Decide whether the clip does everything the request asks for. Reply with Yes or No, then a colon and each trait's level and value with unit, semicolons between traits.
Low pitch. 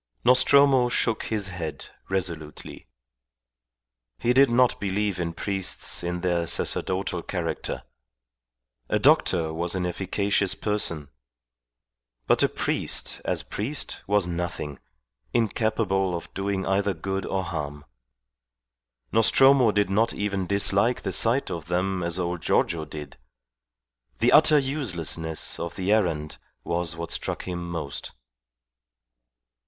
Yes: very low, 95 Hz